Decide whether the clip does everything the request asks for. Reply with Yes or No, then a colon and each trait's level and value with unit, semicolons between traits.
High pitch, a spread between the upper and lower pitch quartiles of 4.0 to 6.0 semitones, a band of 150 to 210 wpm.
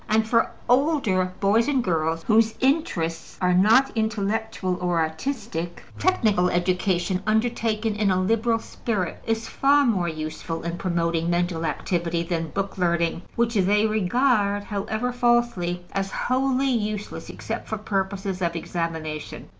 No: high, 200 Hz; average, 4.6 semitones; slow, 135 wpm